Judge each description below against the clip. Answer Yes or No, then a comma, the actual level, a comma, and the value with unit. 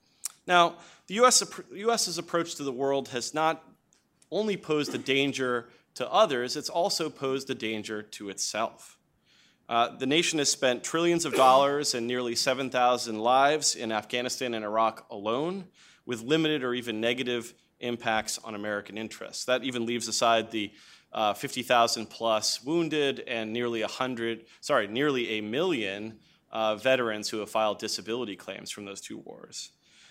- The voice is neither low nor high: No, low, 125 Hz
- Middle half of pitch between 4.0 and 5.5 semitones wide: Yes, average, 4.4 semitones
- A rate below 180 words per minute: Yes, average, 150 wpm